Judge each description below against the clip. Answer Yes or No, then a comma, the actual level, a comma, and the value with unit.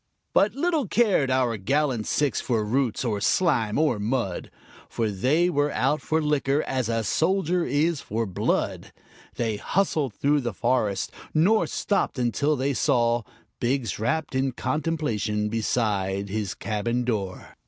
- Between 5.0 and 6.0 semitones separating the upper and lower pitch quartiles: Yes, wide, 5.6 semitones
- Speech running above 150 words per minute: No, average, 145 wpm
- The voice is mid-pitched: No, low, 130 Hz